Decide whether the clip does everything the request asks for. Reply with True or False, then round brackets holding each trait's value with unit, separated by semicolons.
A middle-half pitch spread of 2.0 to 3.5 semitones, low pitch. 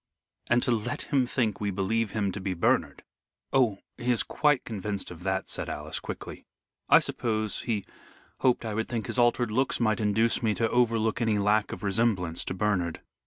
True (2.9 semitones; 110 Hz)